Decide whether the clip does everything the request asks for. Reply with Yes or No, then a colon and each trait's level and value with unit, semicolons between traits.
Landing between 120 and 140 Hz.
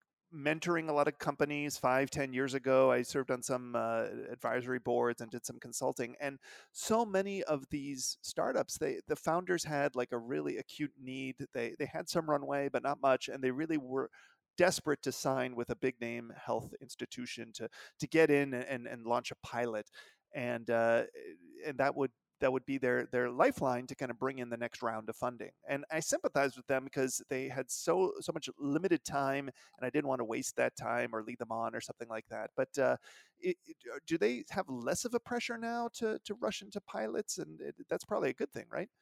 Yes: low, 135 Hz